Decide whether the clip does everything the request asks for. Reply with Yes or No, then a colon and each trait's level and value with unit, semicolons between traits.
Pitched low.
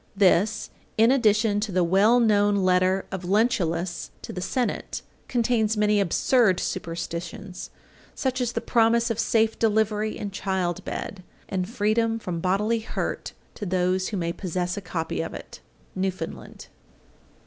No: high, 205 Hz